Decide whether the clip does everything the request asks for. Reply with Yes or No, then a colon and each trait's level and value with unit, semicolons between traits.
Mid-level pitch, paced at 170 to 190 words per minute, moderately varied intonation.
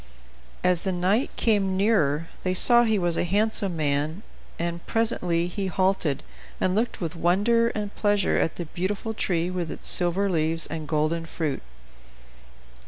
No: medium, 180 Hz; average, 155 wpm; average, 3.7 semitones